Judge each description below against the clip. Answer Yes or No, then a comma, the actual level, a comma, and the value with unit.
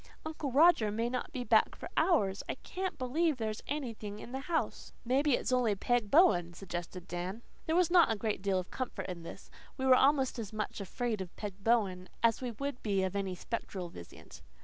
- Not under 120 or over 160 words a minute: No, fast, 205 wpm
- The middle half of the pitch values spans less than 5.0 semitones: No, wide, 5.4 semitones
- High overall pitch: Yes, high, 230 Hz